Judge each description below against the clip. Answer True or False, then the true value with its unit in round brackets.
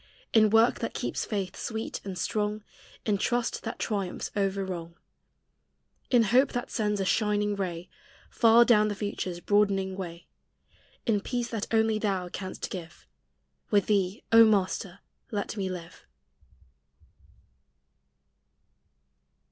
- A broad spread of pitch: False (2.8 semitones)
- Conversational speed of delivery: False (125 wpm)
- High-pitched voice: True (205 Hz)